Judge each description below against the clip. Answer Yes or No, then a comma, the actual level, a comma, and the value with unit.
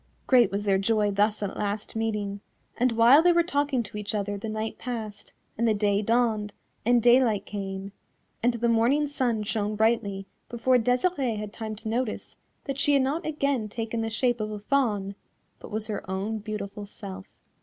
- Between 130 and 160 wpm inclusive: No, average, 185 wpm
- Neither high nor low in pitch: No, high, 220 Hz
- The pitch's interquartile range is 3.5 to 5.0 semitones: No, average, 2.9 semitones